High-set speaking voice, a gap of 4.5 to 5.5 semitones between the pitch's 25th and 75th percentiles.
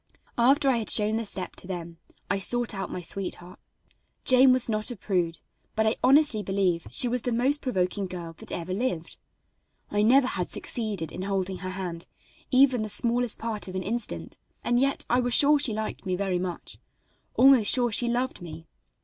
Yes: high, 215 Hz; average, 5.0 semitones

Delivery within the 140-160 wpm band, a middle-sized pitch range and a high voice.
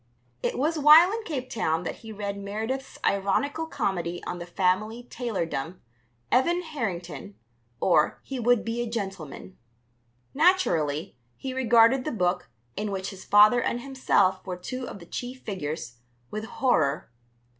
No: average, 145 wpm; wide, 6.0 semitones; high, 215 Hz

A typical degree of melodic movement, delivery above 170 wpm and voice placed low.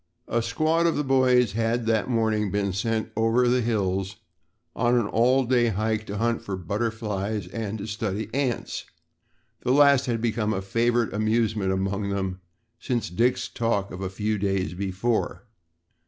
No: average, 3.1 semitones; average, 165 wpm; low, 110 Hz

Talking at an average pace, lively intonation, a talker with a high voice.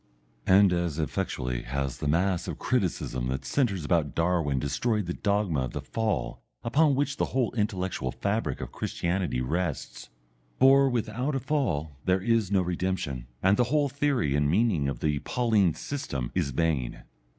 No: average, 160 wpm; wide, 8.2 semitones; very low, 90 Hz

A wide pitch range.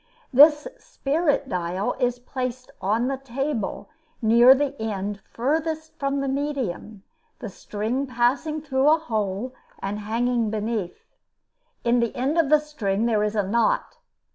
No: average, 4.6 semitones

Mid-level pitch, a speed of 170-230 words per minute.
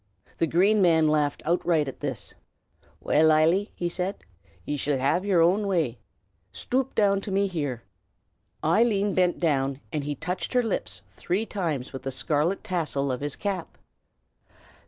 No: medium, 165 Hz; average, 155 wpm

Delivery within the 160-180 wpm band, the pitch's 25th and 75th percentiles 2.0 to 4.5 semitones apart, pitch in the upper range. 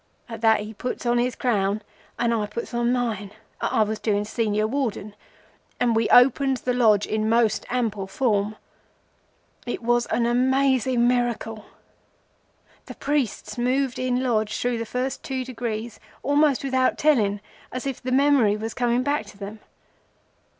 No: average, 150 wpm; average, 2.9 semitones; high, 240 Hz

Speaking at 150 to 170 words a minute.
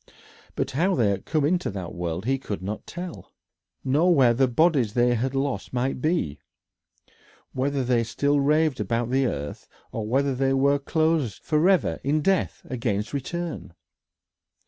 Yes: average, 155 wpm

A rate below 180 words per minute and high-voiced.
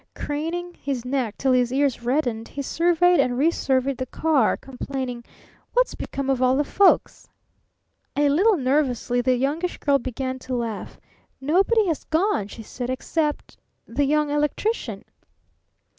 Yes: average, 145 wpm; very high, 275 Hz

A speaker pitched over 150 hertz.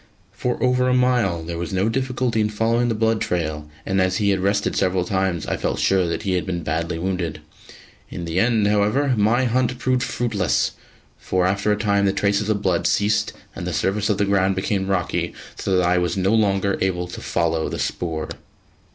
No: low, 100 Hz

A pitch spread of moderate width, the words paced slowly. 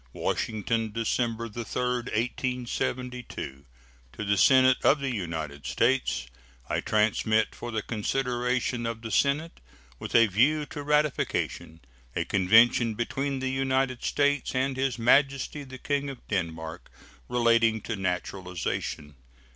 Yes: average, 3.6 semitones; slow, 125 wpm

